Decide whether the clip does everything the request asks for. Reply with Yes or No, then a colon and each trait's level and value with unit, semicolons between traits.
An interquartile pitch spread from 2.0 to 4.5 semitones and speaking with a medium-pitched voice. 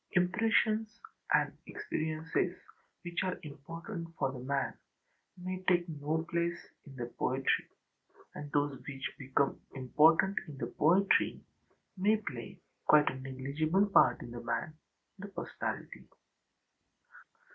No: average, 5.2 semitones; medium, 155 Hz